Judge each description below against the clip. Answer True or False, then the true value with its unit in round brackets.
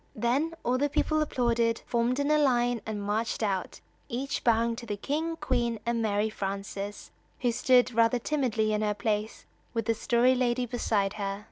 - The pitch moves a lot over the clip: False (2.9 semitones)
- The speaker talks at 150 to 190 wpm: True (170 wpm)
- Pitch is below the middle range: False (235 Hz)